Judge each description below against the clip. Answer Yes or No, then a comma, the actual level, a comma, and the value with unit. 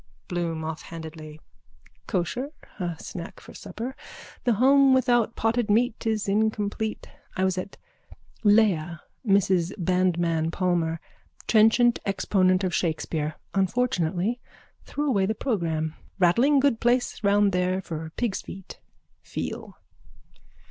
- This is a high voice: Yes, high, 195 Hz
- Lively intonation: No, average, 4.7 semitones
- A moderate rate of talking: No, slow, 115 wpm